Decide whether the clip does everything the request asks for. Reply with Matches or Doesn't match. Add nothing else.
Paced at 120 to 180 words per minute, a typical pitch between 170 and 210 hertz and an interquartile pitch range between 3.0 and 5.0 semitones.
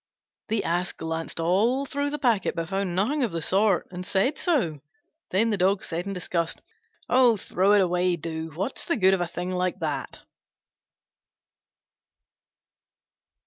Matches